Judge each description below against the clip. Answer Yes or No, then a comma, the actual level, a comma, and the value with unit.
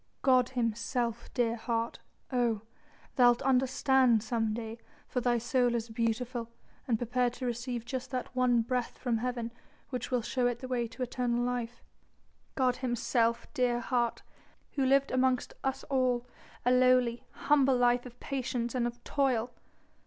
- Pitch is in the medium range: No, high, 245 Hz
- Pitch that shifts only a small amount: Yes, narrow, 1.4 semitones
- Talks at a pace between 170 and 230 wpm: No, average, 150 wpm